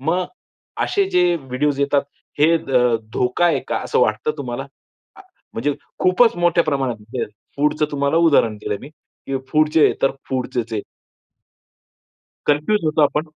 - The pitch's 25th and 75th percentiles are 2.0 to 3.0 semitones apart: No, average, 3.9 semitones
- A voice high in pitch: No, medium, 150 Hz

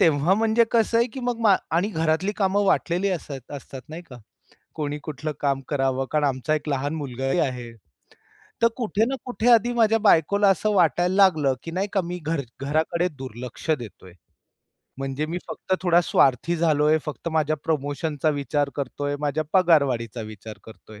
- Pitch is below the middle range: No, medium, 155 Hz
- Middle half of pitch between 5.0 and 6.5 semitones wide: Yes, average, 5.3 semitones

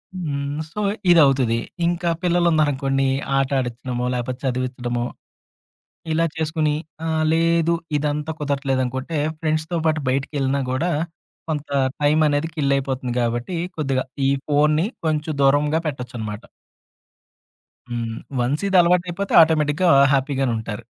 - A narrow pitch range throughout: No, average, 3.5 semitones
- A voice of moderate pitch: Yes, medium, 145 Hz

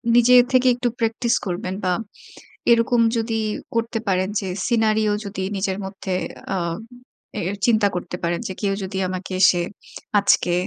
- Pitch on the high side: Yes, high, 205 Hz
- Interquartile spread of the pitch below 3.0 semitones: No, average, 3.5 semitones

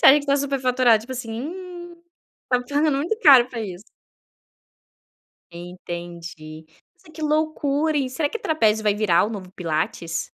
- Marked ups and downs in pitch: Yes, wide, 8.3 semitones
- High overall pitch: Yes, very high, 255 Hz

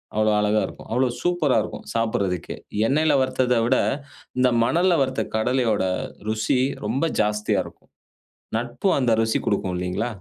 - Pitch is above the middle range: No, low, 120 Hz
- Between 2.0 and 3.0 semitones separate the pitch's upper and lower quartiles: No, average, 3.5 semitones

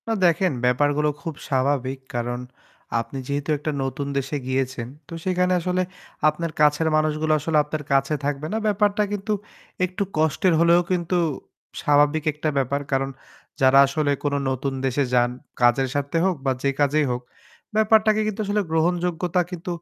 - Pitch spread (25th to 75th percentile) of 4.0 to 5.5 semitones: Yes, average, 4.5 semitones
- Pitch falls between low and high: Yes, medium, 150 Hz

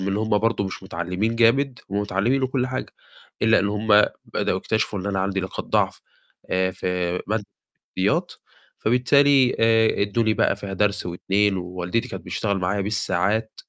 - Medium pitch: No, low, 105 Hz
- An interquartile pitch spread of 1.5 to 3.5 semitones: Yes, average, 3.0 semitones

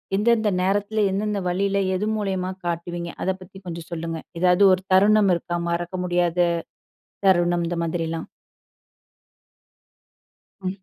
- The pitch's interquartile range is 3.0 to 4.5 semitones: No, narrow, 2.5 semitones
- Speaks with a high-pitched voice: No, medium, 180 Hz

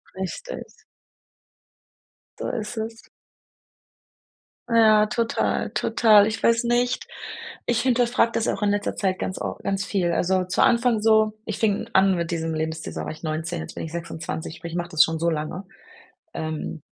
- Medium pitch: No, high, 195 Hz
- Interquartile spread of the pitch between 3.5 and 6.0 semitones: Yes, average, 5.2 semitones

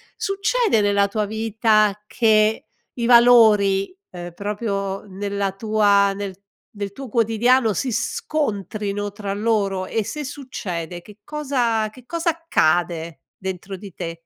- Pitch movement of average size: Yes, average, 3.0 semitones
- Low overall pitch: No, high, 210 Hz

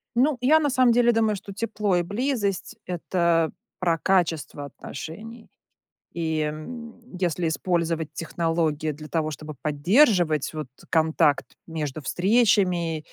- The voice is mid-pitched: Yes, medium, 175 Hz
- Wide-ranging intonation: Yes, wide, 5.8 semitones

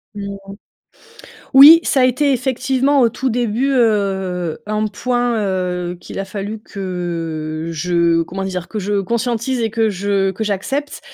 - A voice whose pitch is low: No, high, 205 Hz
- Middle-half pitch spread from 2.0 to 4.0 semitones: No, average, 4.9 semitones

